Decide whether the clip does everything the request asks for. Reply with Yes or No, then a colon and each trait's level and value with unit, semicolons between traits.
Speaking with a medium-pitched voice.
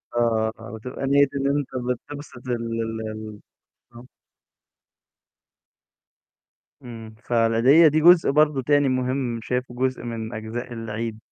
No: low, 120 Hz